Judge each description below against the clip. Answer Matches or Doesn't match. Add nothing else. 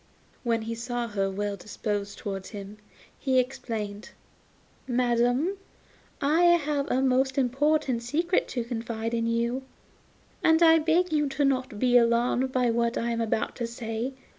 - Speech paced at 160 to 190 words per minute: Doesn't match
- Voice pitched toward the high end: Matches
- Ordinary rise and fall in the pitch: Matches